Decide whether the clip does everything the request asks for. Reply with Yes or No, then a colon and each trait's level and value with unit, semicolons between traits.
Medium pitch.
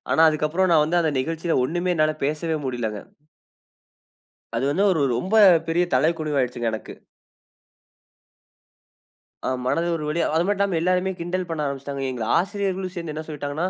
Yes: medium, 160 Hz